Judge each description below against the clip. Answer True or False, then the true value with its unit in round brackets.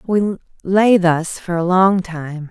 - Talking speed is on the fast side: False (170 wpm)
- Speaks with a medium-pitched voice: True (180 Hz)